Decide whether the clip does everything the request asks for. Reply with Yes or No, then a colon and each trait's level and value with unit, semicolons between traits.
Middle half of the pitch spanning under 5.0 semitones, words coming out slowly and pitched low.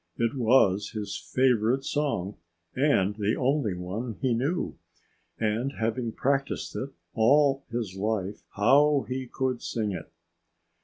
Yes: average, 4.2 semitones; slow, 125 wpm; low, 120 Hz